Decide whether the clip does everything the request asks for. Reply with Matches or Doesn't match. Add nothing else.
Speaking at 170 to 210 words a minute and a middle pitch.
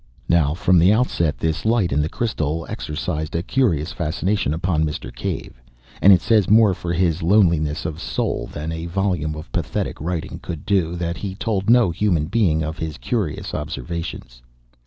Doesn't match